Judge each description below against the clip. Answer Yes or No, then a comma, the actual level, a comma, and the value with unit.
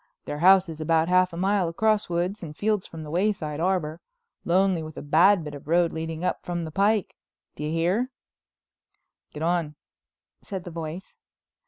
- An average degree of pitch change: Yes, average, 3.1 semitones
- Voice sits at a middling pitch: Yes, medium, 170 Hz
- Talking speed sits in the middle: Yes, average, 180 wpm